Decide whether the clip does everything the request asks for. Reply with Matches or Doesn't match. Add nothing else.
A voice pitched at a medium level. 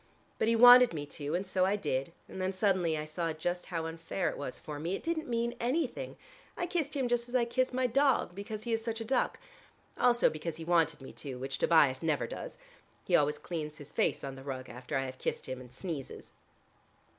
Matches